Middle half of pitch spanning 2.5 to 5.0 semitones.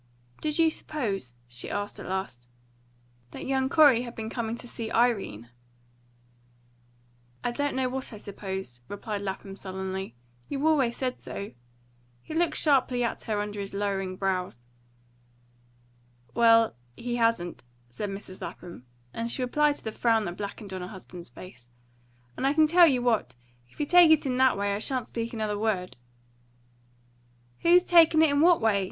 No: wide, 5.4 semitones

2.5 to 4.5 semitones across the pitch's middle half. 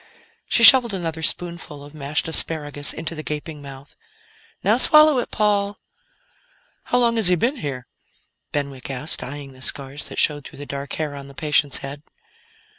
Yes: average, 4.2 semitones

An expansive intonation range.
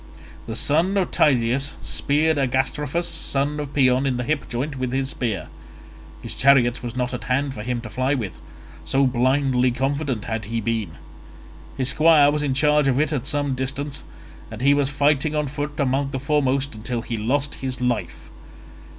No: narrow, 2.6 semitones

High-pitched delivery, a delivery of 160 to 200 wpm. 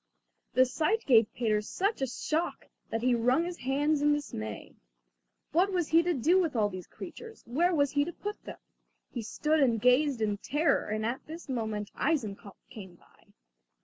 Yes: very high, 270 Hz; average, 180 wpm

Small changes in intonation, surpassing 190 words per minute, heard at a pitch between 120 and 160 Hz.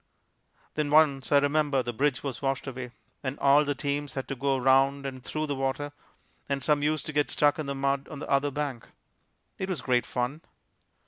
Yes: narrow, 1.6 semitones; fast, 205 wpm; medium, 140 Hz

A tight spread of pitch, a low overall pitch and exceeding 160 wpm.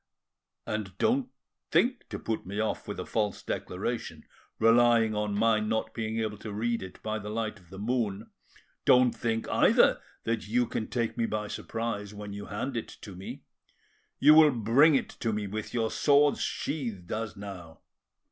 Yes: narrow, 2.3 semitones; low, 110 Hz; average, 175 wpm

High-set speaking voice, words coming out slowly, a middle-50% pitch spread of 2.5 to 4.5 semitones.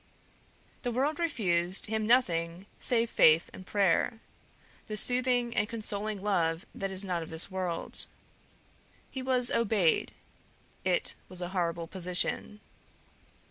No: high, 195 Hz; slow, 125 wpm; average, 4.9 semitones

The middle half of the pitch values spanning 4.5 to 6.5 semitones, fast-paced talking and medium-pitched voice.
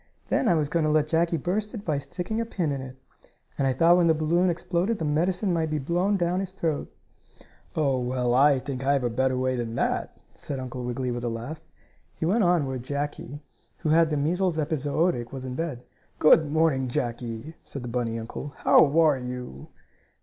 Yes: average, 4.8 semitones; fast, 210 wpm; medium, 150 Hz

